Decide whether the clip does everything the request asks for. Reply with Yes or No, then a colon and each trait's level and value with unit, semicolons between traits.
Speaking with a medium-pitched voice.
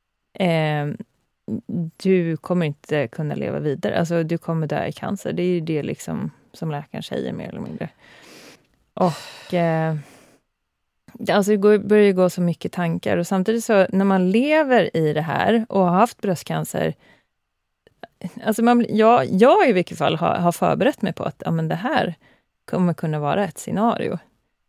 Yes: medium, 180 Hz